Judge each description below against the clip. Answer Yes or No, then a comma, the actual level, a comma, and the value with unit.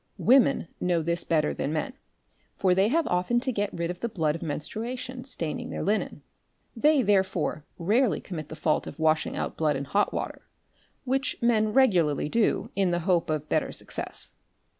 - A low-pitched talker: No, medium, 185 Hz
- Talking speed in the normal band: Yes, average, 180 wpm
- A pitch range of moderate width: No, wide, 6.8 semitones